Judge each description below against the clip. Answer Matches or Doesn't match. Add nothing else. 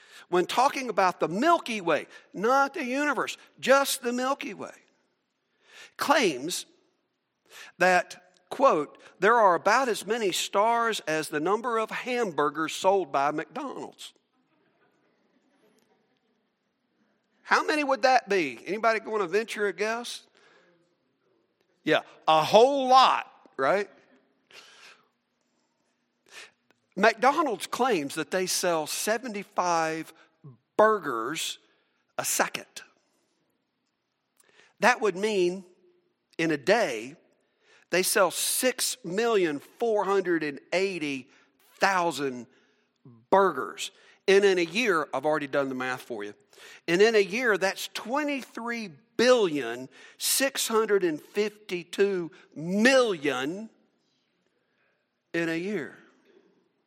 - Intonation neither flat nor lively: Doesn't match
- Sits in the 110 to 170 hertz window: Doesn't match